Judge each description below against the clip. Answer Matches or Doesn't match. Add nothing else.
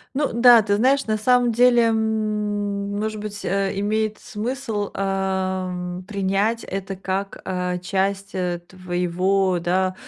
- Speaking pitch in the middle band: Doesn't match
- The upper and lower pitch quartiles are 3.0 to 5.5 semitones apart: Doesn't match